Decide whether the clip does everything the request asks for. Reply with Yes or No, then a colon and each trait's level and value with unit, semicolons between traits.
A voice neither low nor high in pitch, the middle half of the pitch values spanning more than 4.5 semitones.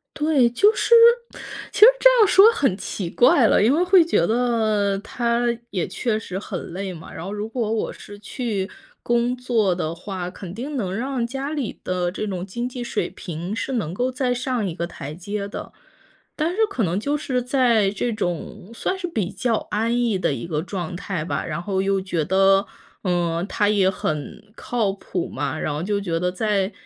No: high, 205 Hz; average, 5.0 semitones